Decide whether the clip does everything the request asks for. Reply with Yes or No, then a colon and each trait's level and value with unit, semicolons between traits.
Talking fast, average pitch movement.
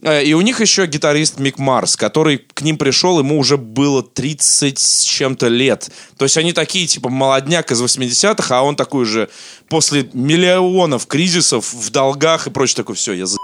Yes: fast, 185 wpm; average, 3.7 semitones